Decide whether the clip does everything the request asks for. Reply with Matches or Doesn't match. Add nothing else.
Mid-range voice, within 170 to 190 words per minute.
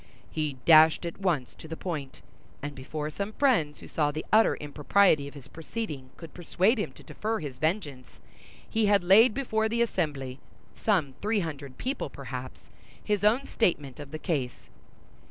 Doesn't match